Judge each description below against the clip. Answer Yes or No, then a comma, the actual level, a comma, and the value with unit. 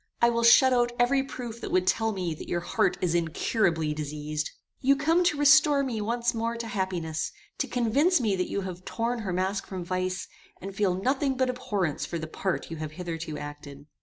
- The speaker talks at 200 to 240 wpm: Yes, fast, 205 wpm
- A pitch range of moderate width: No, wide, 6.0 semitones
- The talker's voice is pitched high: Yes, high, 195 Hz